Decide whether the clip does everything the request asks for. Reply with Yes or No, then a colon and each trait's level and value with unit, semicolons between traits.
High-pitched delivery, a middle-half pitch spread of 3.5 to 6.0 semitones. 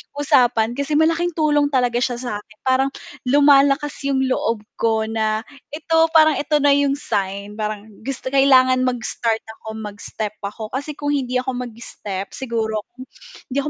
Yes: very high, 255 Hz; average, 4.5 semitones